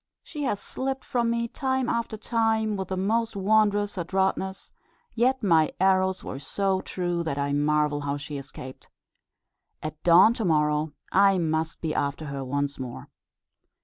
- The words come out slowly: No, average, 155 wpm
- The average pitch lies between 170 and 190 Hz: Yes, medium, 185 Hz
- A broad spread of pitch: Yes, wide, 6.4 semitones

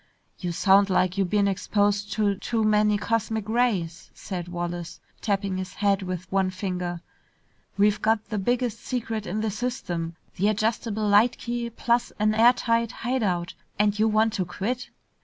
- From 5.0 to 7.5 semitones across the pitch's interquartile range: No, average, 3.1 semitones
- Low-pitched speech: No, high, 205 Hz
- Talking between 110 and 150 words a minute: No, average, 160 wpm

